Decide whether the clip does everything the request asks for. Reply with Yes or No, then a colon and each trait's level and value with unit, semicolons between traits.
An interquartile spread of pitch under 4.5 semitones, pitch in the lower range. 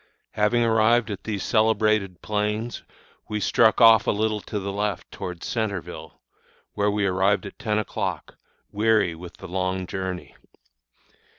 Yes: narrow, 2.4 semitones; low, 105 Hz